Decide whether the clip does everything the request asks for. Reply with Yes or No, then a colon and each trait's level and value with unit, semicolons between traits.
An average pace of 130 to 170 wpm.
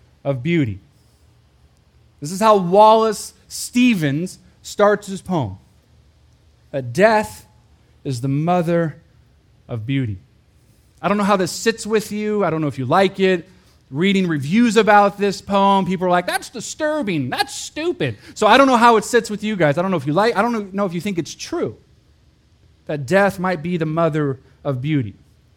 No: average, 180 wpm